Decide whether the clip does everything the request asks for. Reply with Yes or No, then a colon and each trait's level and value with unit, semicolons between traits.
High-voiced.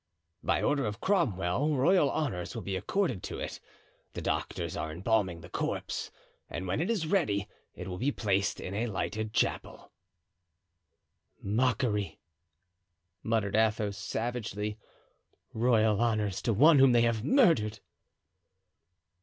No: low, 110 Hz